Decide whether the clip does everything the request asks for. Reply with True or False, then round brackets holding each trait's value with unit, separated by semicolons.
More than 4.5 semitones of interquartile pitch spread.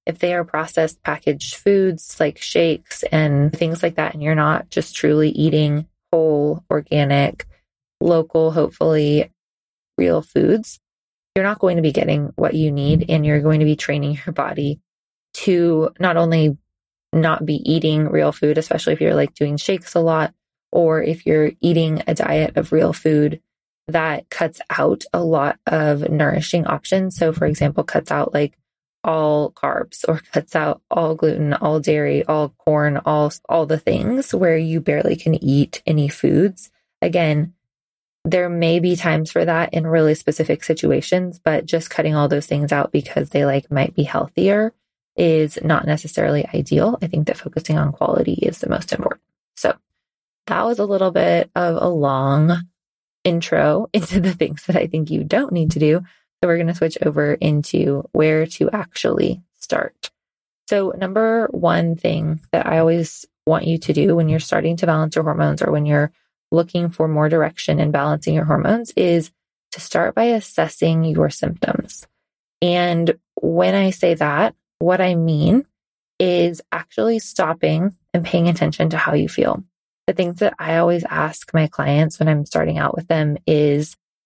False (2.4 semitones)